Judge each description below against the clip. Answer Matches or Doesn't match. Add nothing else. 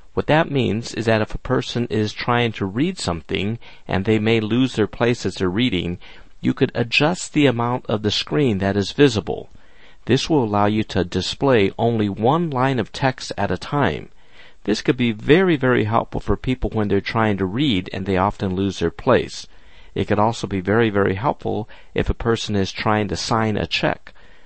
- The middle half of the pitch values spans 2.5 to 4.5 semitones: Matches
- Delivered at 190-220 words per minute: Matches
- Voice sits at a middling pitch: Doesn't match